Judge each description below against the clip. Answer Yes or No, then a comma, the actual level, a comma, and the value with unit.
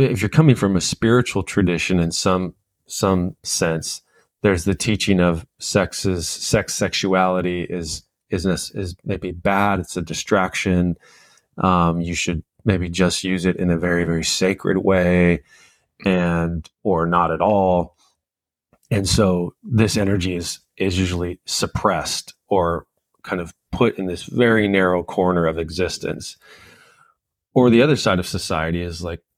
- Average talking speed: Yes, average, 145 wpm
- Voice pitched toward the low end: Yes, very low, 90 Hz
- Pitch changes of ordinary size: No, narrow, 2.3 semitones